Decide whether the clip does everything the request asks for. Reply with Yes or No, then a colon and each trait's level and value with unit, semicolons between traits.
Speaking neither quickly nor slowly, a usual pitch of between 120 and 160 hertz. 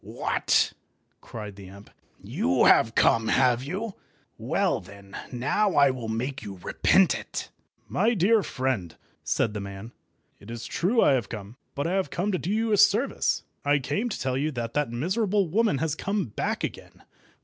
Yes: average, 175 wpm; low, 135 Hz